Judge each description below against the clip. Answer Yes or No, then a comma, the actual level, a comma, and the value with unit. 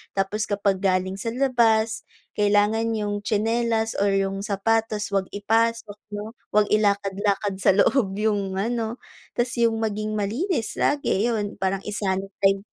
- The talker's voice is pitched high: Yes, high, 210 Hz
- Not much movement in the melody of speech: Yes, narrow, 2.3 semitones